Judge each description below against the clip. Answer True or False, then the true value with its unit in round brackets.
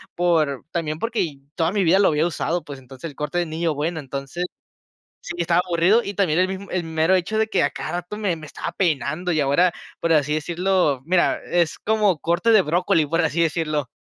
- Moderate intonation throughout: True (3.0 semitones)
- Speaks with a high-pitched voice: False (170 Hz)